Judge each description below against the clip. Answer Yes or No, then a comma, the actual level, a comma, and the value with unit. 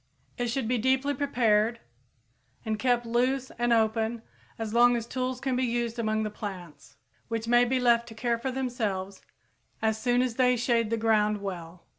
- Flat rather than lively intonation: Yes, narrow, 2.3 semitones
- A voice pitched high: Yes, high, 235 Hz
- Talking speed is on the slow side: No, average, 180 wpm